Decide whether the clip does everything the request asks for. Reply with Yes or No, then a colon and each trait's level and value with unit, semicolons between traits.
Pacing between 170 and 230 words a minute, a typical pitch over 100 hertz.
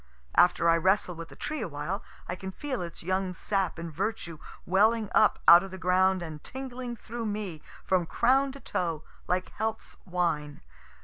Yes: average, 175 wpm; medium, 185 Hz